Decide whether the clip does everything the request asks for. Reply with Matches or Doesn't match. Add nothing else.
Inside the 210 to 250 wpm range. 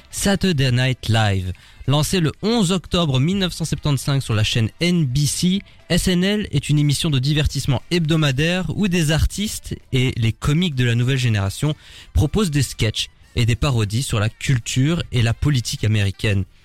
Doesn't match